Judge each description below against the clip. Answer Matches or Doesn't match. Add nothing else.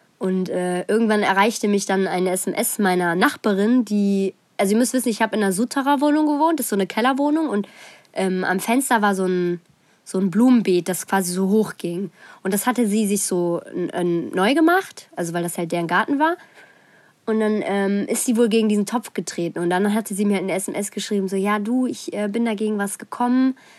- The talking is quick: Matches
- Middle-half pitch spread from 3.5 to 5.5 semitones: Matches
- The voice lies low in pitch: Doesn't match